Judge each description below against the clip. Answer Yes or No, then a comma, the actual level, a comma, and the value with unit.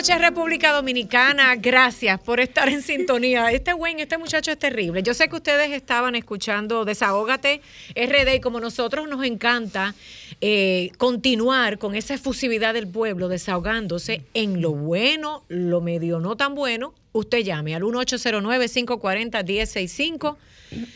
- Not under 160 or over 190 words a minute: No, average, 135 wpm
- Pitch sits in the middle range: No, high, 240 Hz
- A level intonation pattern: No, average, 4.7 semitones